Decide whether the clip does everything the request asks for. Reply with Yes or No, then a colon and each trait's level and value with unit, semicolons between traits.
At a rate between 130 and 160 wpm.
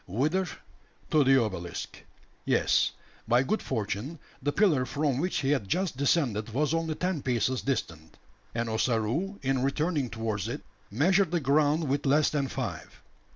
Yes: average, 155 wpm